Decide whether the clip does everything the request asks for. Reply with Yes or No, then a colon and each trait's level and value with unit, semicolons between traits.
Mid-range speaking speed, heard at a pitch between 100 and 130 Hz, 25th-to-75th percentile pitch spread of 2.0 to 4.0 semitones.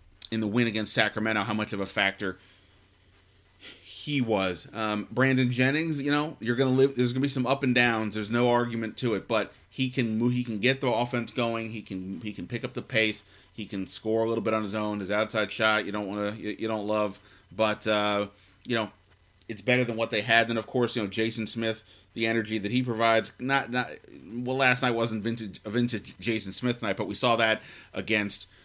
No: fast, 225 wpm; low, 110 Hz; average, 2.8 semitones